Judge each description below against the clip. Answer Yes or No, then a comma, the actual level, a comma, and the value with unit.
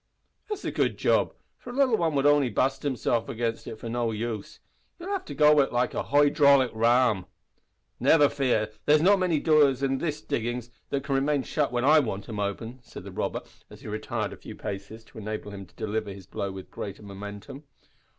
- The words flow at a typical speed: No, fast, 215 wpm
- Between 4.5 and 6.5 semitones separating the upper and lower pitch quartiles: Yes, average, 5.2 semitones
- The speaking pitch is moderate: No, low, 125 Hz